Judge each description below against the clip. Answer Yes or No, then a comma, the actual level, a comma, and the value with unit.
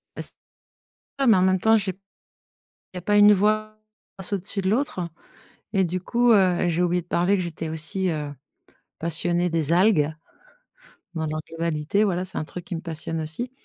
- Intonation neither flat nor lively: Yes, average, 3.6 semitones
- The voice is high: No, medium, 180 Hz